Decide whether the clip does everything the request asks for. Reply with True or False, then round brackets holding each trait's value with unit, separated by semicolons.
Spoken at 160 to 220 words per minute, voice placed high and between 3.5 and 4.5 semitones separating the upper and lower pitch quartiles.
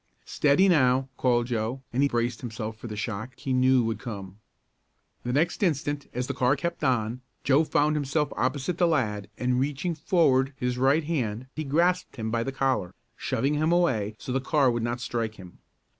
False (190 wpm; 130 Hz; 3.9 semitones)